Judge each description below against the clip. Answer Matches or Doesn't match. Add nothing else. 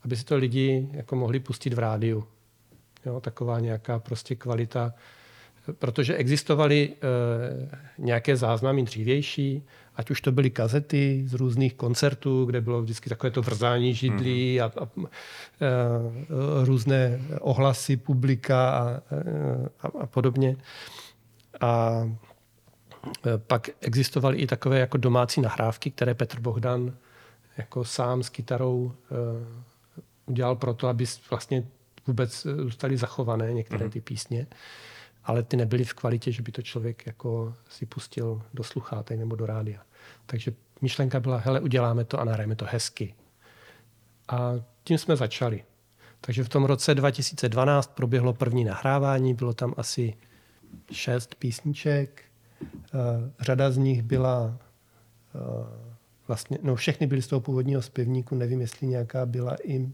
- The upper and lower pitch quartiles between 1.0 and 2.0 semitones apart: Doesn't match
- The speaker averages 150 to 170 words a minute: Doesn't match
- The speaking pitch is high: Doesn't match